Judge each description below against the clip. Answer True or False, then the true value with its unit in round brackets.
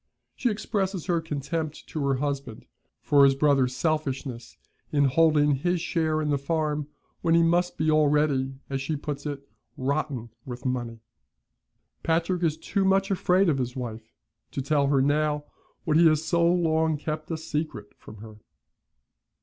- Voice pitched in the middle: True (150 Hz)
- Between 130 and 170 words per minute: True (160 wpm)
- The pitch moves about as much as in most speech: True (3.1 semitones)